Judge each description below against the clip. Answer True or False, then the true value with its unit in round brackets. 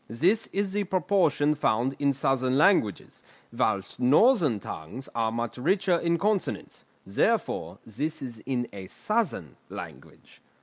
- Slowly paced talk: True (130 wpm)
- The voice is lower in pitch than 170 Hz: True (140 Hz)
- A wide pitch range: True (8.0 semitones)